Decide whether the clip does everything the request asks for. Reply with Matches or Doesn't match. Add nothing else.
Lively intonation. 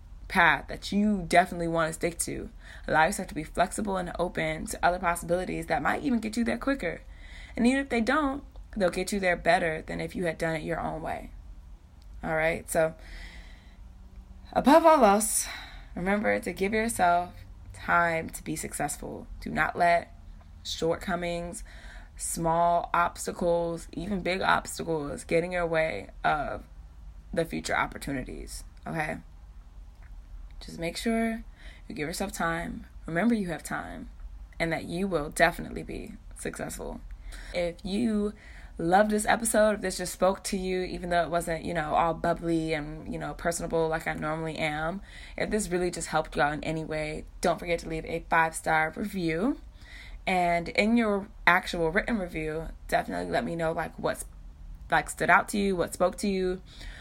Doesn't match